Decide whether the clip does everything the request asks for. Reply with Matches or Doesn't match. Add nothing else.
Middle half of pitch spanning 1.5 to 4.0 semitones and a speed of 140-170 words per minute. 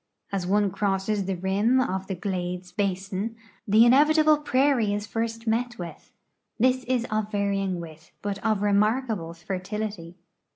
Matches